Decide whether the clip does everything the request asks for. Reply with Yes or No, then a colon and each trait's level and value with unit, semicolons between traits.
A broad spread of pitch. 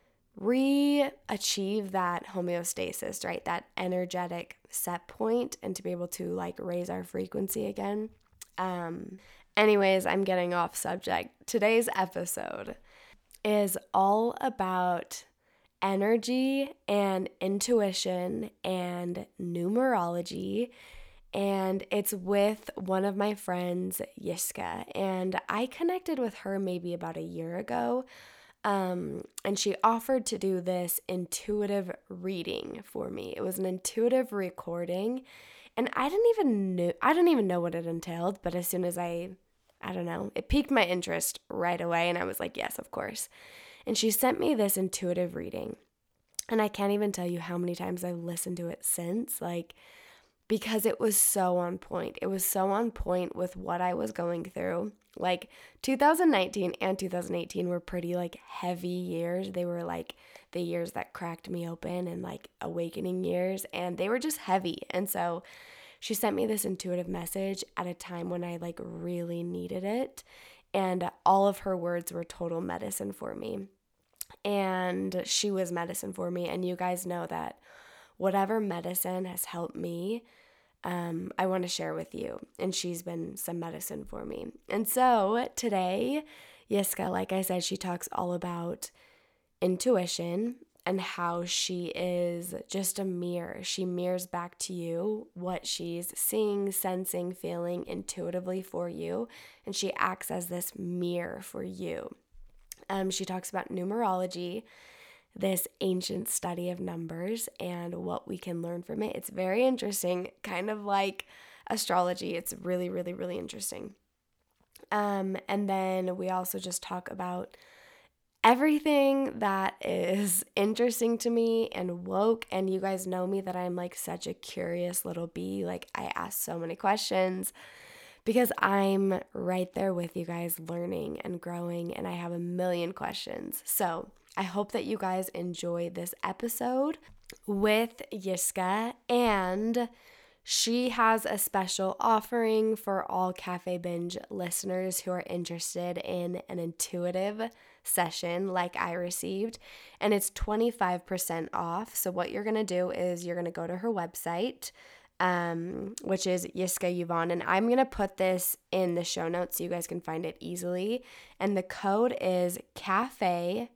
No: average, 3.4 semitones